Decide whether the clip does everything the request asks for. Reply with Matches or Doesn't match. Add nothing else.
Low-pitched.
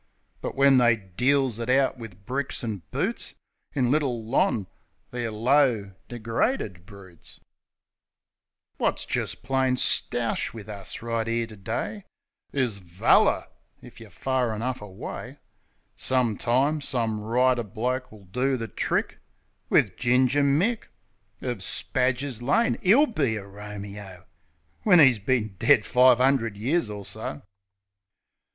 Matches